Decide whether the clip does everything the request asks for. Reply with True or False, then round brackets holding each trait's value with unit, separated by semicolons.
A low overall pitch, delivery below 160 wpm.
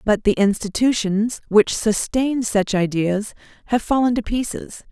False (220 Hz; 135 wpm)